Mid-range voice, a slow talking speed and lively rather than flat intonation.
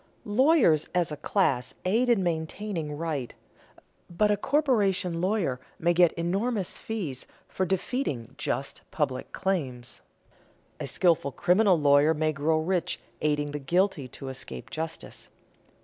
No: medium, 170 Hz; slow, 130 wpm; average, 4.9 semitones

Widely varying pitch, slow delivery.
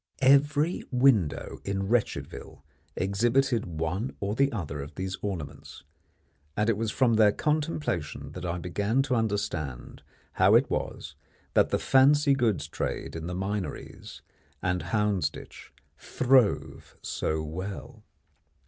Yes: wide, 6.1 semitones; slow, 120 wpm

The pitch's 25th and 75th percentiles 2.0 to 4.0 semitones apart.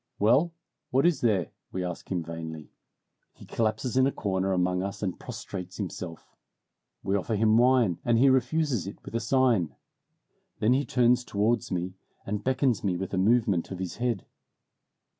No: average, 5.1 semitones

